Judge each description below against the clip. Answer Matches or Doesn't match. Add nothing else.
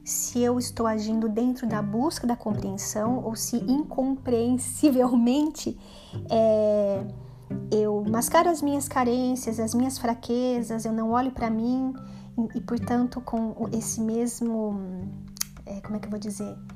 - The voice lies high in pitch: Matches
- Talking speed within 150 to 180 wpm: Doesn't match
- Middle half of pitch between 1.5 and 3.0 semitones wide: Matches